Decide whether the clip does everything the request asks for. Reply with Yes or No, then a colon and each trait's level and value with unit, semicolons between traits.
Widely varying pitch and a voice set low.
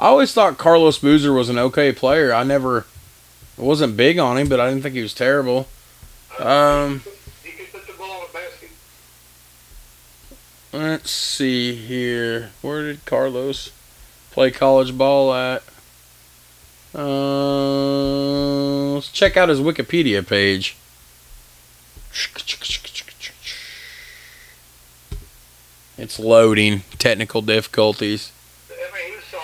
Yes: wide, 7.2 semitones; low, 130 Hz